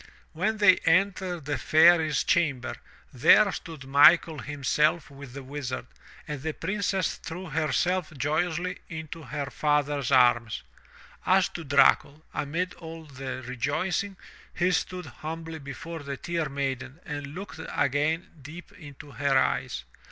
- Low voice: No, medium, 155 Hz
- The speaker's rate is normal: No, slow, 130 wpm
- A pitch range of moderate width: Yes, average, 3.7 semitones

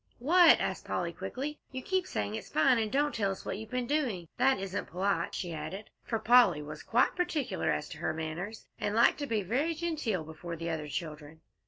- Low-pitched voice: No, high, 210 Hz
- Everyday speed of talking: No, fast, 210 wpm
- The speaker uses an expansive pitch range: Yes, wide, 8.2 semitones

